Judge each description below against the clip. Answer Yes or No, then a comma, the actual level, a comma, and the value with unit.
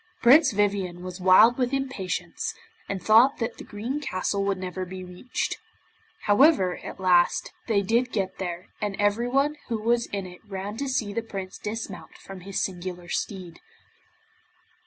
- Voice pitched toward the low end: No, high, 200 Hz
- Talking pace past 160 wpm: No, average, 155 wpm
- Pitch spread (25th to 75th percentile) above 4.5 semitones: No, average, 4.2 semitones